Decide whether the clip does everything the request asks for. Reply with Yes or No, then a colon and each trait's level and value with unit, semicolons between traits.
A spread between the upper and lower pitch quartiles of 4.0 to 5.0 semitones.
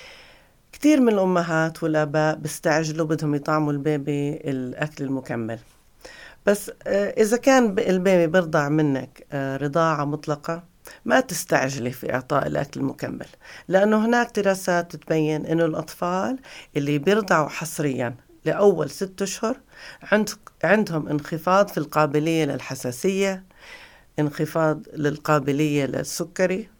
Yes: average, 4.6 semitones